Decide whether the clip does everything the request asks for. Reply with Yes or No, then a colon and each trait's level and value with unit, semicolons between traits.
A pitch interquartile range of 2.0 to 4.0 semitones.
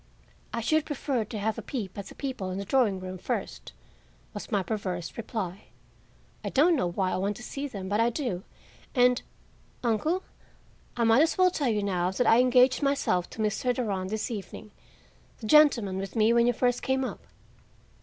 No: average, 4.6 semitones